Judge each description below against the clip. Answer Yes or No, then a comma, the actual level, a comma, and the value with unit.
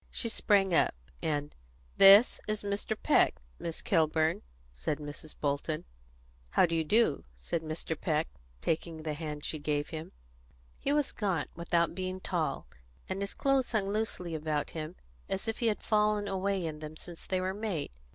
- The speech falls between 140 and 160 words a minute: No, average, 170 wpm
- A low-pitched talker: No, medium, 170 Hz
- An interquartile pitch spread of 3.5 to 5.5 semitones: Yes, average, 4.4 semitones